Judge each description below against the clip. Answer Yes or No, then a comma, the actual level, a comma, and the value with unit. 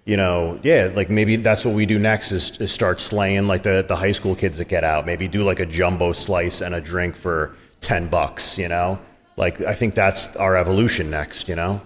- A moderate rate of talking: No, fast, 235 wpm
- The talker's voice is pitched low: Yes, very low, 95 Hz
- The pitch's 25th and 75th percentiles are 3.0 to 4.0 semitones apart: No, narrow, 2.6 semitones